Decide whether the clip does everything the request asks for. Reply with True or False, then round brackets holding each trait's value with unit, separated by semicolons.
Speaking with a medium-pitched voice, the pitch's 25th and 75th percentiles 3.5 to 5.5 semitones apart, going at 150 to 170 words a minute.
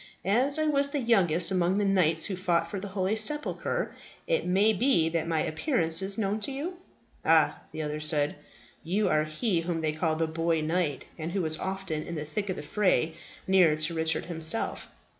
False (175 Hz; 4.3 semitones; 200 wpm)